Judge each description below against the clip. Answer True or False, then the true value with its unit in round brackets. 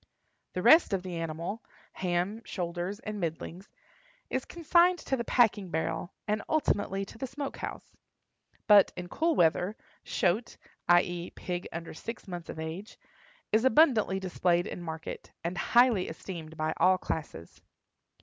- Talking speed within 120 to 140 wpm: True (135 wpm)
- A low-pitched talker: False (185 Hz)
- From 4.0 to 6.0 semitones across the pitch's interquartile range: True (5.1 semitones)